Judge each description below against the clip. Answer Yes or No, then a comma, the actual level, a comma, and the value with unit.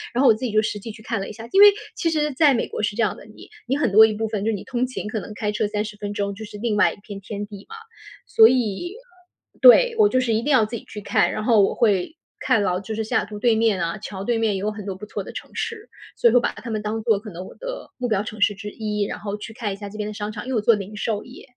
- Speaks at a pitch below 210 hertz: No, high, 215 Hz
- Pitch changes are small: Yes, narrow, 2.2 semitones